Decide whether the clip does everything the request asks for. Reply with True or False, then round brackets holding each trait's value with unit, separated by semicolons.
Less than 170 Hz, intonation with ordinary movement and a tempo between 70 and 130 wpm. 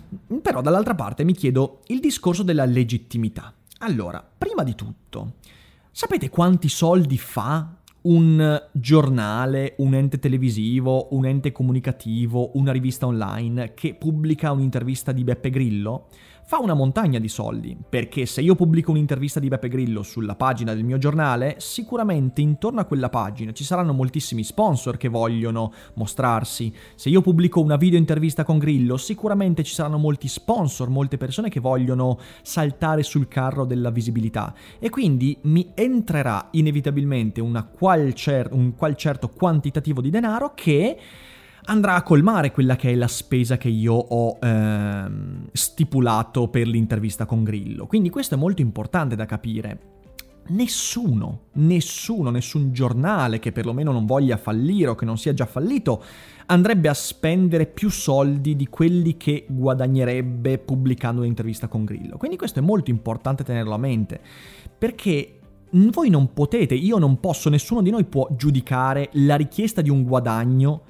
False (135 Hz; 4.8 semitones; 150 wpm)